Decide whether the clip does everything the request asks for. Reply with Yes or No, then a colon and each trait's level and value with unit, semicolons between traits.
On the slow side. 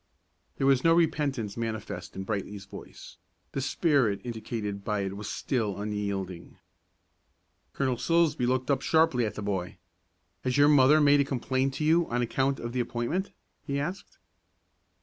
No: average, 155 wpm